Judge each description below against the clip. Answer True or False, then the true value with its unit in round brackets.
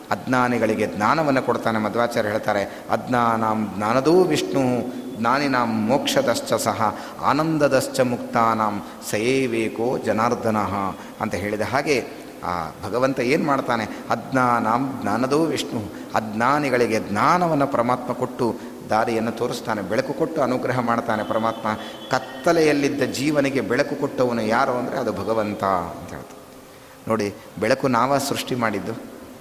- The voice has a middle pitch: False (120 Hz)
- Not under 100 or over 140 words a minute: True (105 wpm)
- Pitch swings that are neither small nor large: True (3.0 semitones)